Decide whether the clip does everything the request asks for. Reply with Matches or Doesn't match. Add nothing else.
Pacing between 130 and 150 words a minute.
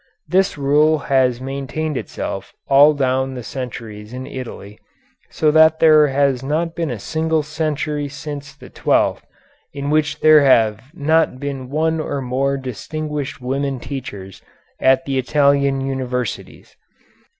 Matches